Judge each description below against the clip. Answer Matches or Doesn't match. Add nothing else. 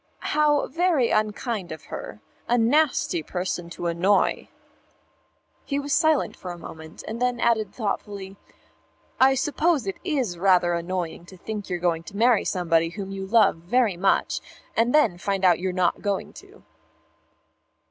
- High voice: Matches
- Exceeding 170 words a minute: Doesn't match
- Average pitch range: Doesn't match